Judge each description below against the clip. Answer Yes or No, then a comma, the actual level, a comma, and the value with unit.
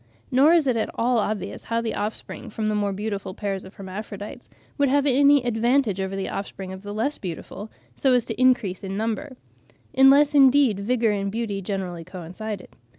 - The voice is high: Yes, high, 215 Hz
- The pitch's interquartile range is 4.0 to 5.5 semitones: Yes, average, 4.5 semitones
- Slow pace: No, average, 185 wpm